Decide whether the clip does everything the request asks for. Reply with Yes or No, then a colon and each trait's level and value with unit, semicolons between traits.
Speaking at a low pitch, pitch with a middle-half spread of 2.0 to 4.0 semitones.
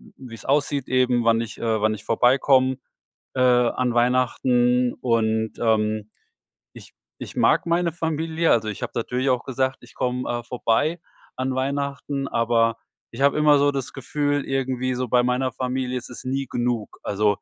Yes: low, 125 Hz; narrow, 2.5 semitones